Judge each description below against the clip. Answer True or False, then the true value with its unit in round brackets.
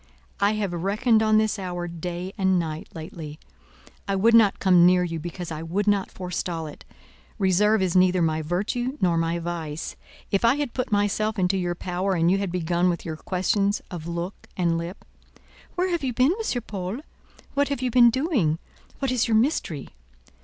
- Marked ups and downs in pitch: False (4.1 semitones)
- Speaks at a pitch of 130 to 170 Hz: False (185 Hz)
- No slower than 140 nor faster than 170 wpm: False (185 wpm)